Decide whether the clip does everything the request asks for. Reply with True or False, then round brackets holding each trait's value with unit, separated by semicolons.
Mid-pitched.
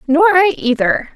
False (315 Hz)